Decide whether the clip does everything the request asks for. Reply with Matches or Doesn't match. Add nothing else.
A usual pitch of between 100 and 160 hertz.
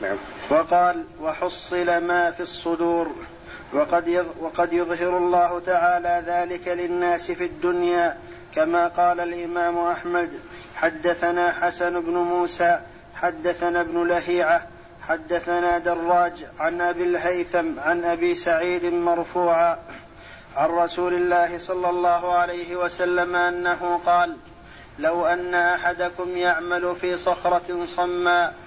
Doesn't match